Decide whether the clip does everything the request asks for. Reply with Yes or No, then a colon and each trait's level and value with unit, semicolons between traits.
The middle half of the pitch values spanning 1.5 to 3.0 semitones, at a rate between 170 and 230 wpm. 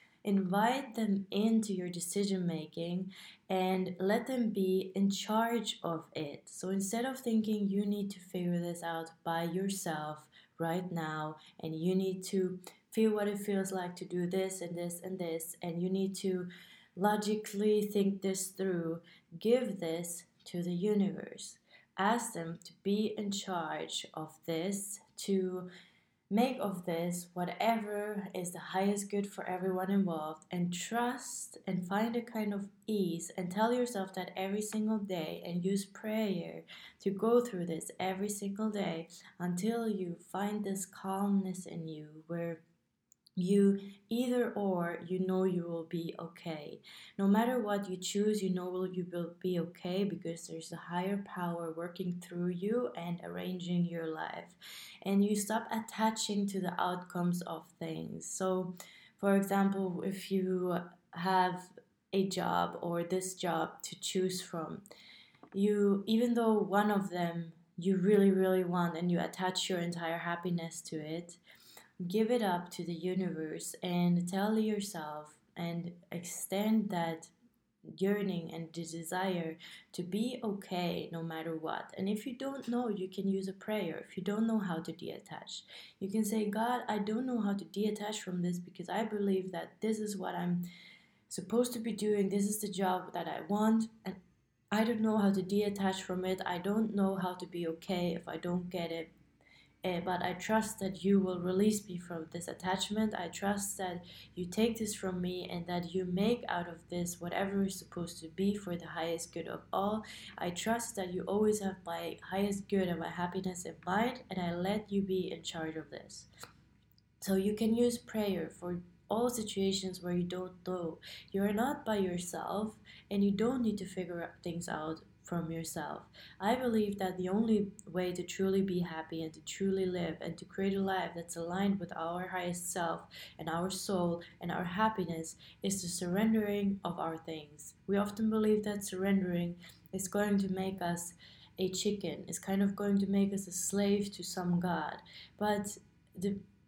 Yes: average, 2.7 semitones; average, 175 wpm